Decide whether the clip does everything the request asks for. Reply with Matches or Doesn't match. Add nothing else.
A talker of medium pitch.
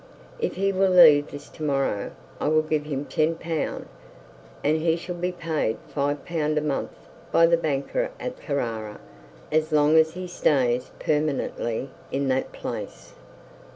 Matches